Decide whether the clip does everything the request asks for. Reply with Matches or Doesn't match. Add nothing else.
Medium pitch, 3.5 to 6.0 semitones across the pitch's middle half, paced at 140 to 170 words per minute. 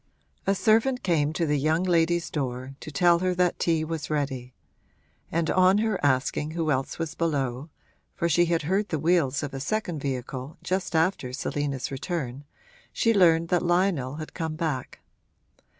Matches